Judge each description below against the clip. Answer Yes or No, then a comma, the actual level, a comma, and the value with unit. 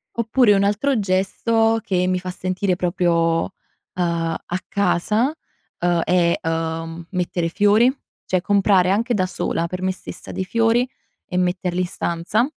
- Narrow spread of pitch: No, average, 3.1 semitones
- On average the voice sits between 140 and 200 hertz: Yes, medium, 185 Hz